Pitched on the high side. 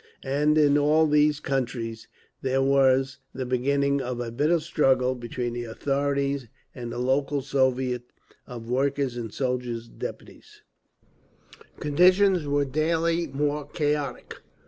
No: low, 135 Hz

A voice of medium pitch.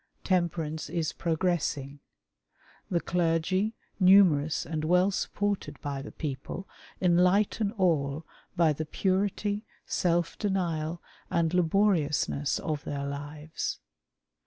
Yes: medium, 170 Hz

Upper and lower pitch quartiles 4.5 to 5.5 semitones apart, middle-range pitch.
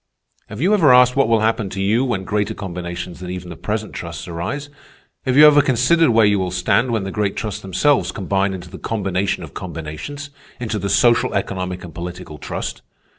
No: average, 5.2 semitones; low, 100 Hz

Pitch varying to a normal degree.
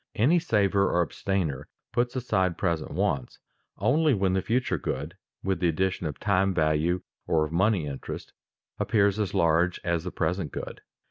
Yes: average, 3.7 semitones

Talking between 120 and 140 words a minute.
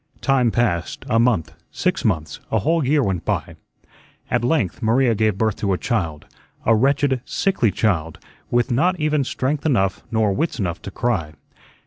No: average, 165 wpm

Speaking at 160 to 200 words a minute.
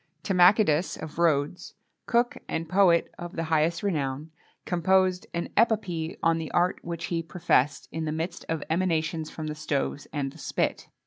Yes: average, 165 wpm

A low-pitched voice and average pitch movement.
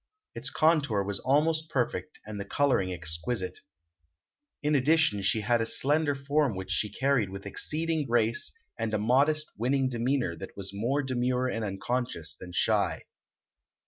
No: low, 120 Hz; wide, 5.9 semitones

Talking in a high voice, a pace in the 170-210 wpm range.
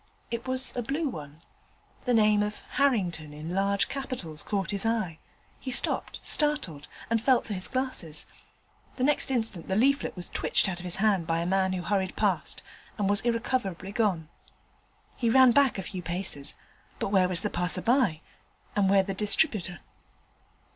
Yes: high, 200 Hz; average, 175 wpm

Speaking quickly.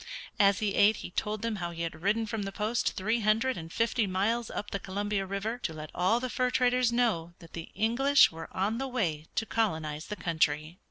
Yes: fast, 220 wpm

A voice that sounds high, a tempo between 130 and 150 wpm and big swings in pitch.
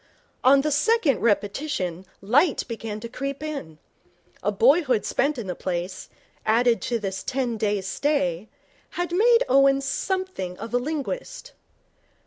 Yes: very high, 255 Hz; slow, 135 wpm; wide, 6.5 semitones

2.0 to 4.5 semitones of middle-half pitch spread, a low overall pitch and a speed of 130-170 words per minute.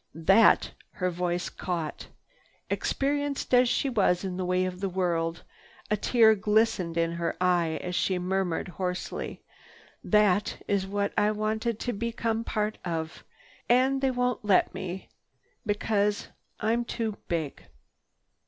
No: average, 3.8 semitones; high, 200 Hz; average, 140 wpm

